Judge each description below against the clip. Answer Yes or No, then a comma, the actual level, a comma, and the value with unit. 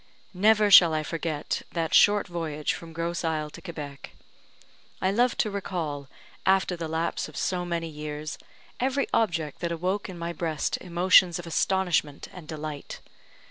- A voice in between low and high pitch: Yes, medium, 170 Hz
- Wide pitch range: No, average, 3.2 semitones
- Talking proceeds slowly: No, average, 155 wpm